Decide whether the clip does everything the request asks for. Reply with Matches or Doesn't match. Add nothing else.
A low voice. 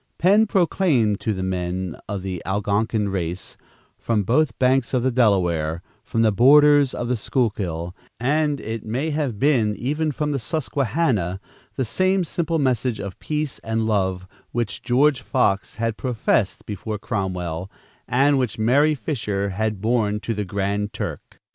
Matches